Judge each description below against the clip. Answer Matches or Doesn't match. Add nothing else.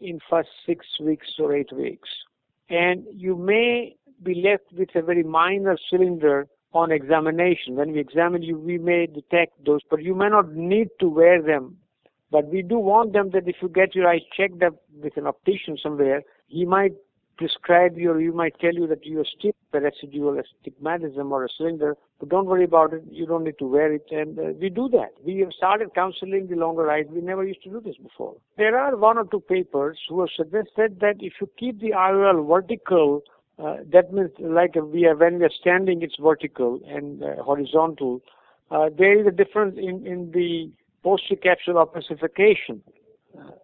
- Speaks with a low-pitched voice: Doesn't match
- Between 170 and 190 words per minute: Doesn't match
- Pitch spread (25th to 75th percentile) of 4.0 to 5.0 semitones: Doesn't match